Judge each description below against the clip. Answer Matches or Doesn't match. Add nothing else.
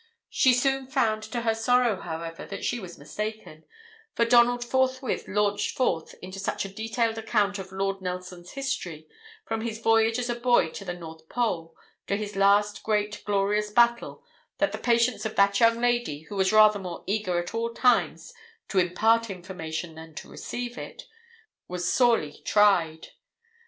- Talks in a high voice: Matches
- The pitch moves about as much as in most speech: Matches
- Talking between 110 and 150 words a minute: Doesn't match